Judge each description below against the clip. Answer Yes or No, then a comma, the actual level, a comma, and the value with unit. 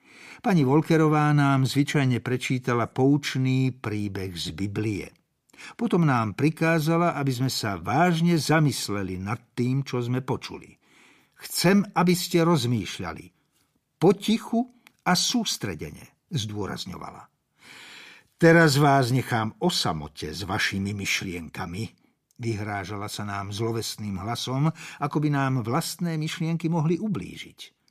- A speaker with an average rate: No, slow, 105 wpm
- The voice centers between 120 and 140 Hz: Yes, low, 135 Hz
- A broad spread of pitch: Yes, wide, 7.2 semitones